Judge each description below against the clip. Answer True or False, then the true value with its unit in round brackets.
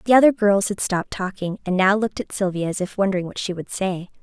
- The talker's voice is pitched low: False (195 Hz)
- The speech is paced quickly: True (255 wpm)